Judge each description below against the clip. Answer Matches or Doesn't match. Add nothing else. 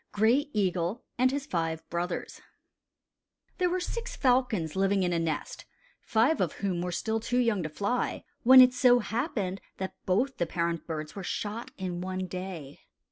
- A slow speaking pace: Doesn't match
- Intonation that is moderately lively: Doesn't match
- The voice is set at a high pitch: Matches